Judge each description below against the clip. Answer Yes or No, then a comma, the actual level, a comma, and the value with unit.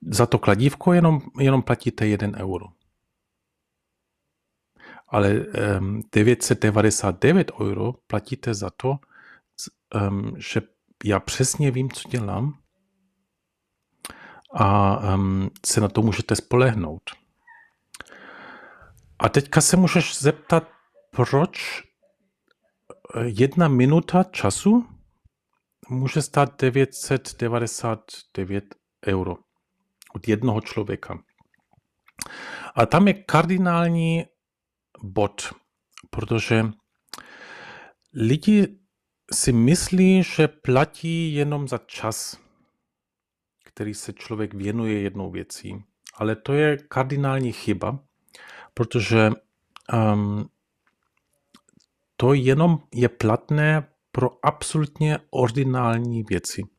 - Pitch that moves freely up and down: Yes, wide, 6.3 semitones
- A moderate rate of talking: No, slow, 80 wpm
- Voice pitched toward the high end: No, low, 125 Hz